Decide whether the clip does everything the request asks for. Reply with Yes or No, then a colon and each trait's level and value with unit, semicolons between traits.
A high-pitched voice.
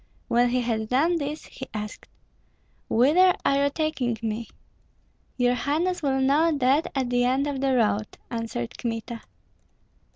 Yes: very high, 260 Hz